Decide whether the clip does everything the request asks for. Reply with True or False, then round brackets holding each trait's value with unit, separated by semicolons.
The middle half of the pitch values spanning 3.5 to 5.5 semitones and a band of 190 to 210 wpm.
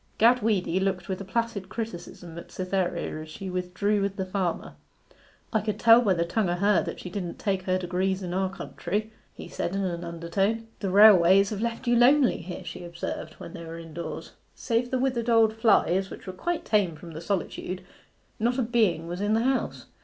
True (4.0 semitones; 205 wpm)